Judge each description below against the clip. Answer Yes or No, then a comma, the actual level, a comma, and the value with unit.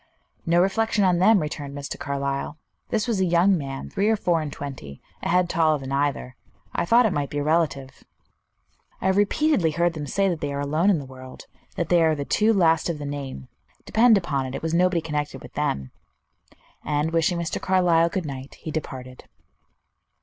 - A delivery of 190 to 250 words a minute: Yes, average, 200 wpm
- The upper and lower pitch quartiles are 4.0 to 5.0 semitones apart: Yes, average, 4.3 semitones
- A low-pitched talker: No, medium, 160 Hz